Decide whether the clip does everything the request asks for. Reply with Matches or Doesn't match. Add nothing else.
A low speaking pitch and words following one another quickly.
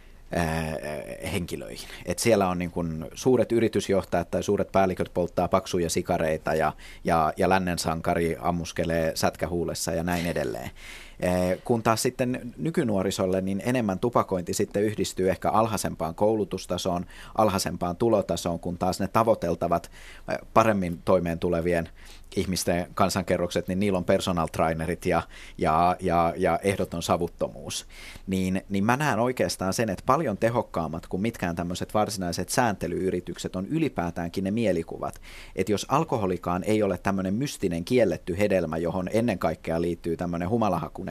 Doesn't match